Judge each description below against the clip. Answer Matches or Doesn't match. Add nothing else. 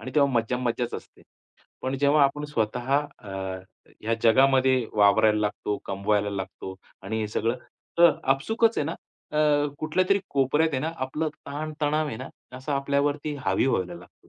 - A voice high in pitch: Doesn't match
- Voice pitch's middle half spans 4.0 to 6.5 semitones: Matches